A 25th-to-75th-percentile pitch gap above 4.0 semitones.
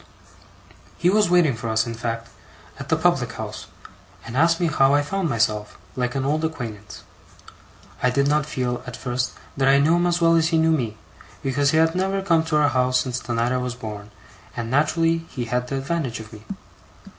Yes: average, 5.2 semitones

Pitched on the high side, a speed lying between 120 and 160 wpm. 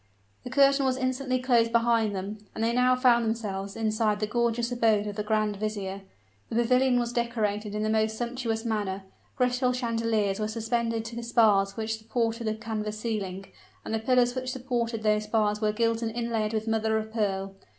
No: high, 225 Hz; average, 190 wpm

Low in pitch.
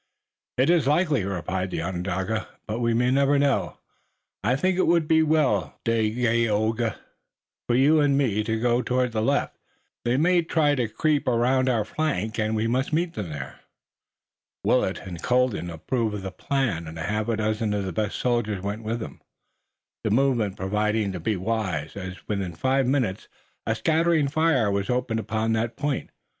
Yes: low, 115 Hz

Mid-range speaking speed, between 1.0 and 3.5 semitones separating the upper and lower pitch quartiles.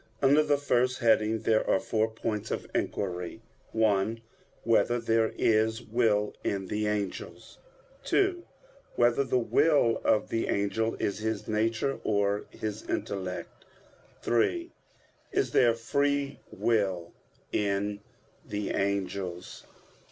No: slow, 115 wpm; average, 2.7 semitones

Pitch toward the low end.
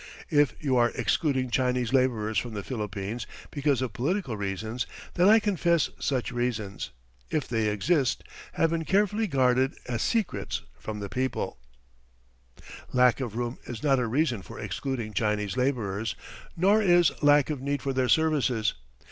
Yes: low, 125 Hz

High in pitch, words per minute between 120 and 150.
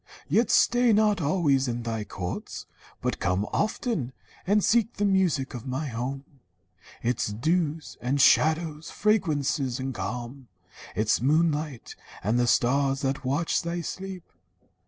No: medium, 145 Hz; slow, 135 wpm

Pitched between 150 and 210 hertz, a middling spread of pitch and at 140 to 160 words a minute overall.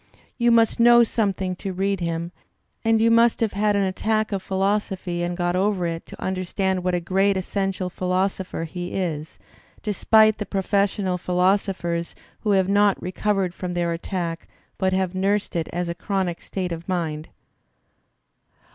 No: high, 190 Hz; narrow, 2.3 semitones; average, 155 wpm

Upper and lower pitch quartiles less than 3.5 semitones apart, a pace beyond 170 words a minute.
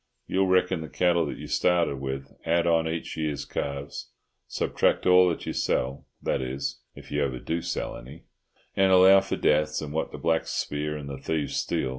No: average, 3.8 semitones; average, 185 wpm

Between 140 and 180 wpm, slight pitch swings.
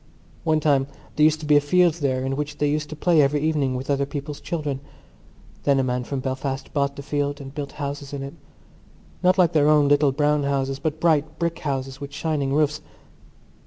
No: average, 200 wpm; narrow, 1.8 semitones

